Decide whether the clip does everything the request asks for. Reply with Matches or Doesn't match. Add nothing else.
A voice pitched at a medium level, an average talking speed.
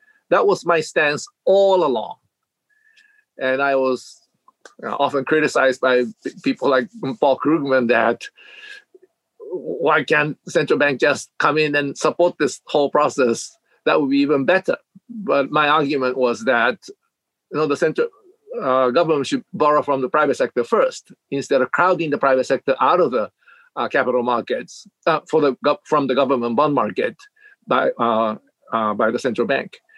Matches